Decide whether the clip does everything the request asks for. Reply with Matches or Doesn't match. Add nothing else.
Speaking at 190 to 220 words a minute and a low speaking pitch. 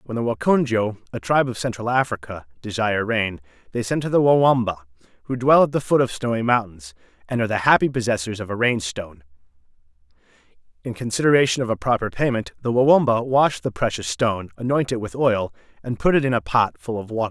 Matches